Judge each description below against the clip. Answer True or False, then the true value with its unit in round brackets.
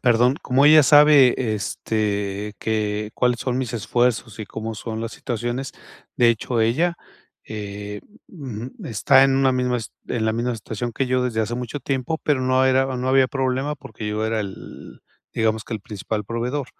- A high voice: False (120 Hz)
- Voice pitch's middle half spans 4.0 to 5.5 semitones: False (3.1 semitones)